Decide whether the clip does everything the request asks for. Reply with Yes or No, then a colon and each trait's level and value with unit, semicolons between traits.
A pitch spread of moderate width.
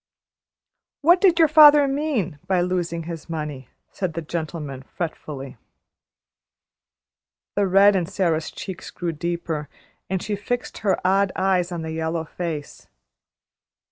Yes: average, 3.8 semitones